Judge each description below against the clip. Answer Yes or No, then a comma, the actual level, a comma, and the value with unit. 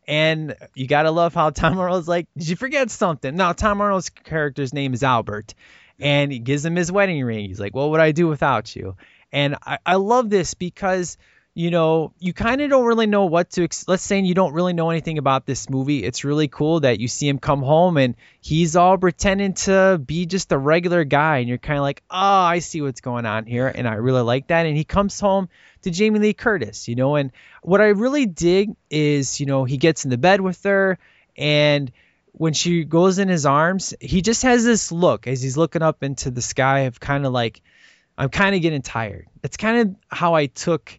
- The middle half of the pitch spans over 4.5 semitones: Yes, average, 5.3 semitones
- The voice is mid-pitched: Yes, medium, 160 Hz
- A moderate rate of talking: No, fast, 225 wpm